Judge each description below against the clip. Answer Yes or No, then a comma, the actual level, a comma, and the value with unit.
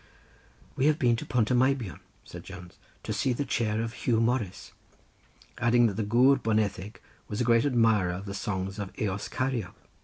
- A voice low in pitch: Yes, low, 115 Hz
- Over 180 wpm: Yes, average, 190 wpm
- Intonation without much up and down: No, average, 3.3 semitones